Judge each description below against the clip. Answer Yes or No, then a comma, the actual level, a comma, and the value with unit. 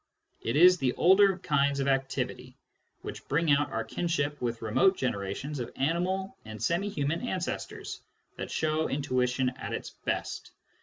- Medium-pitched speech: Yes, medium, 145 Hz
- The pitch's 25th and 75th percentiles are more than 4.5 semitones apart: Yes, average, 4.9 semitones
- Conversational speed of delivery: Yes, average, 150 wpm